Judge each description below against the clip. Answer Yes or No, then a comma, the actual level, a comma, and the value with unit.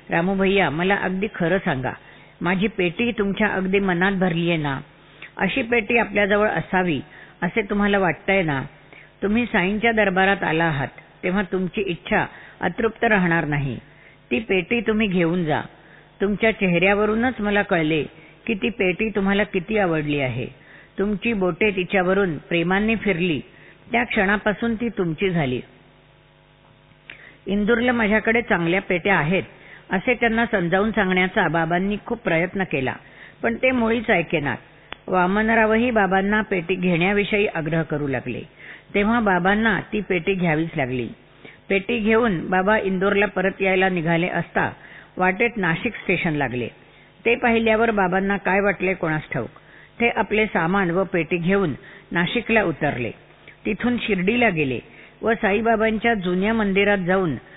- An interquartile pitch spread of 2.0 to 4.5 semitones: Yes, average, 3.9 semitones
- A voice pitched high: Yes, high, 195 Hz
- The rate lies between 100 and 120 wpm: No, fast, 130 wpm